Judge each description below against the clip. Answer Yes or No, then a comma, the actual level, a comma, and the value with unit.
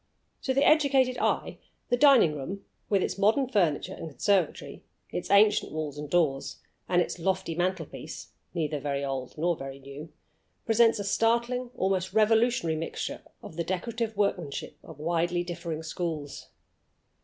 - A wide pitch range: Yes, wide, 6.1 semitones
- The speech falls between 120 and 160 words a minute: Yes, average, 150 wpm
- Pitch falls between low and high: Yes, medium, 175 Hz